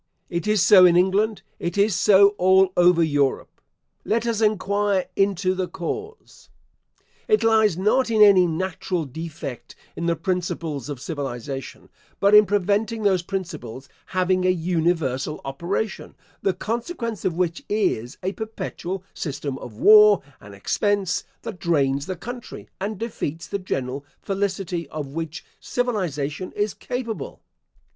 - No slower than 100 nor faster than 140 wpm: Yes, slow, 135 wpm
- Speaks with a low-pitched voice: No, medium, 185 Hz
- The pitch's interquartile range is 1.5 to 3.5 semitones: No, average, 4.3 semitones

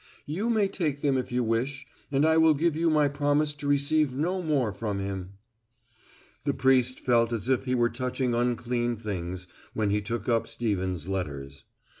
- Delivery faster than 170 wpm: Yes, average, 180 wpm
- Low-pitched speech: Yes, low, 125 Hz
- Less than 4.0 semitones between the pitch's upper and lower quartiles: No, average, 5.1 semitones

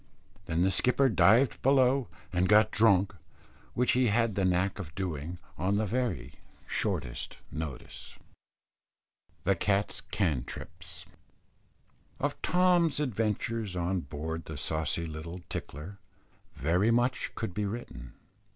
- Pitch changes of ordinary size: No, wide, 5.7 semitones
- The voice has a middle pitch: No, low, 100 Hz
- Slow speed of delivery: Yes, slow, 120 wpm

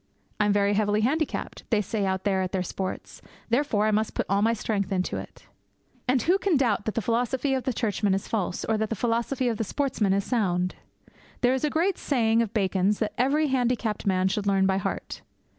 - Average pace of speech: No, fast, 220 wpm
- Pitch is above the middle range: Yes, high, 215 Hz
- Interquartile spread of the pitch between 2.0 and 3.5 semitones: No, average, 3.9 semitones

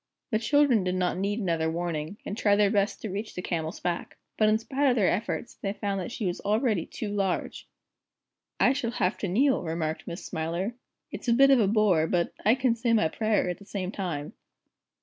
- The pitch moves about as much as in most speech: Yes, average, 4.3 semitones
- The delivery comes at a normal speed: No, fast, 215 wpm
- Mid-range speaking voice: No, high, 200 Hz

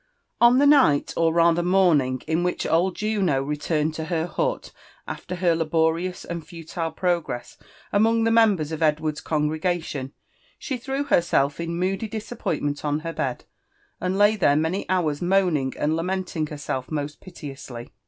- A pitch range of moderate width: Yes, average, 3.7 semitones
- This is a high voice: No, medium, 165 Hz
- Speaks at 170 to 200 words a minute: No, average, 155 wpm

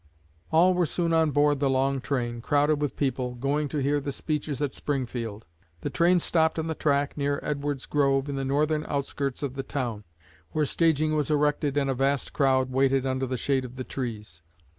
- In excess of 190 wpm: Yes, average, 200 wpm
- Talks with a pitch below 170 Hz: Yes, medium, 140 Hz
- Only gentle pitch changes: Yes, narrow, 2.1 semitones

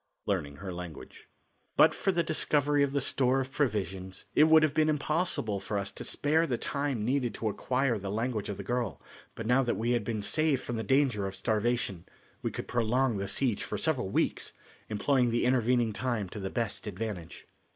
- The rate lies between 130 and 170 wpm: No, average, 200 wpm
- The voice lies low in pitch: Yes, low, 120 Hz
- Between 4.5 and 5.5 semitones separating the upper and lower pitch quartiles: Yes, average, 5.0 semitones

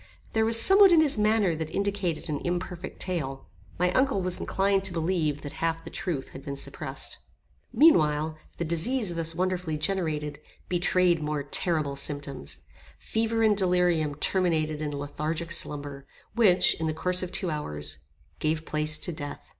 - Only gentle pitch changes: No, average, 3.7 semitones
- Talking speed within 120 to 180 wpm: Yes, average, 160 wpm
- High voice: No, medium, 170 Hz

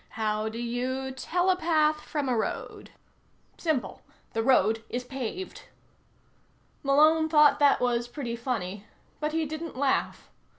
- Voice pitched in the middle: No, very high, 265 Hz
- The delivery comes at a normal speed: No, slow, 125 wpm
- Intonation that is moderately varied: Yes, average, 4.7 semitones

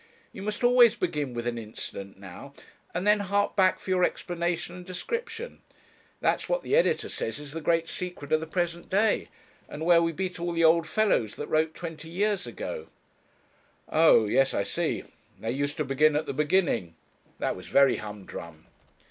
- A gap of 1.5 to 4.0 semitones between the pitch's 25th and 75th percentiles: No, average, 5.1 semitones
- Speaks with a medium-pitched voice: Yes, medium, 165 Hz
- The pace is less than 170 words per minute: No, average, 180 wpm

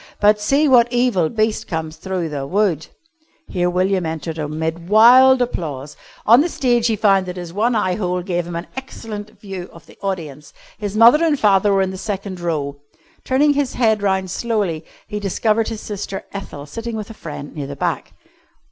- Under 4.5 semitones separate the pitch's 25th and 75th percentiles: No, average, 4.8 semitones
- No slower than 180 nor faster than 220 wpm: Yes, average, 190 wpm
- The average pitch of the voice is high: Yes, high, 195 Hz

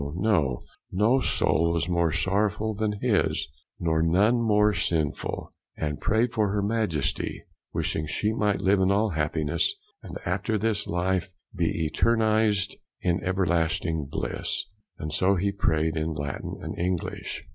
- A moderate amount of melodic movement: Yes, average, 4.4 semitones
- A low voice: Yes, very low, 95 Hz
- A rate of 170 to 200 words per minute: No, slow, 135 wpm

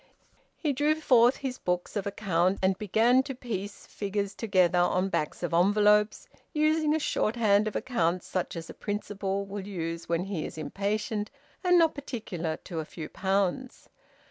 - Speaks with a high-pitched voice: Yes, high, 200 Hz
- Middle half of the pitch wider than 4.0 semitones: Yes, average, 4.7 semitones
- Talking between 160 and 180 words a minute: Yes, average, 165 wpm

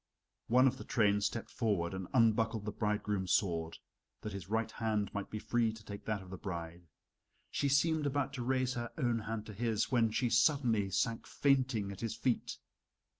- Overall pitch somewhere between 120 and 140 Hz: No, low, 110 Hz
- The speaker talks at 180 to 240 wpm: Yes, average, 190 wpm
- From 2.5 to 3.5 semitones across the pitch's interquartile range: Yes, average, 3.1 semitones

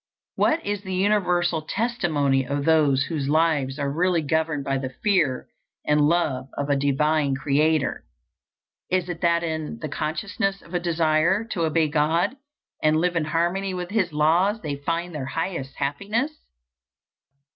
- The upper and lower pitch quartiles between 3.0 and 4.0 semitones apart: Yes, average, 3.6 semitones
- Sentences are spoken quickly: No, average, 155 wpm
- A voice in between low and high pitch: Yes, medium, 160 Hz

